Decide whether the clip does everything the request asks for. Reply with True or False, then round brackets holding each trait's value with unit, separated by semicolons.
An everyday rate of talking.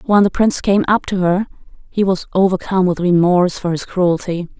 True (195 wpm)